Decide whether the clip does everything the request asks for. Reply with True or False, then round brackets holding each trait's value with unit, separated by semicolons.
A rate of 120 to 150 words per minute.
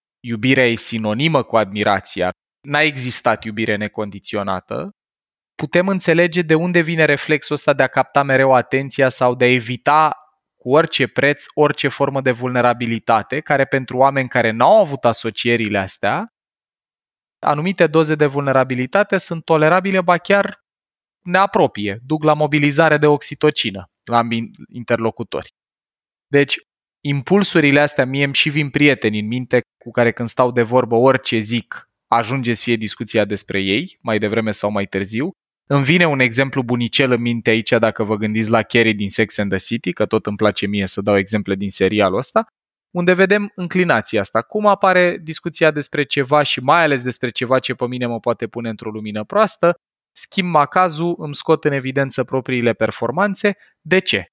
False (160 wpm)